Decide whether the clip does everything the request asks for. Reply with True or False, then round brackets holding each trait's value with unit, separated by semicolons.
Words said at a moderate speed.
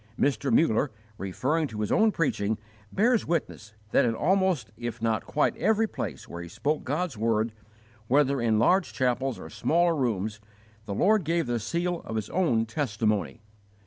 True (165 wpm)